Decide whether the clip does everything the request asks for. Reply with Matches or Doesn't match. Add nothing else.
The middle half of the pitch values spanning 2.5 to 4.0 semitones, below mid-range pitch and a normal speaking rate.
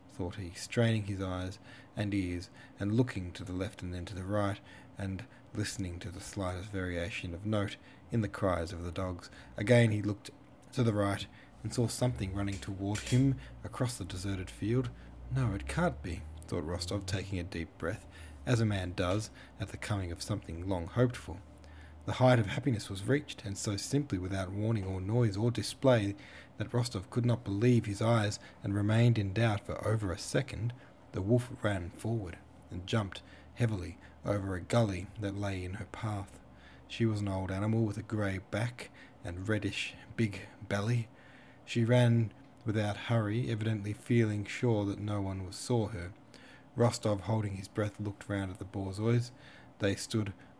Matches